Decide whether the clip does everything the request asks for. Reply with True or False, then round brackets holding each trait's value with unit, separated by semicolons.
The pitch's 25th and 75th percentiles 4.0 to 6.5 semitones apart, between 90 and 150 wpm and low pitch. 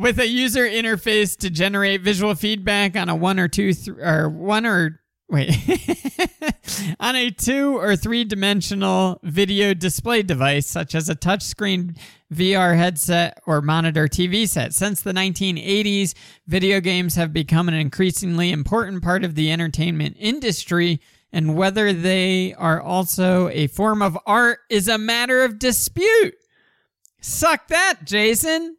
False (4.4 semitones; 145 wpm; 195 Hz)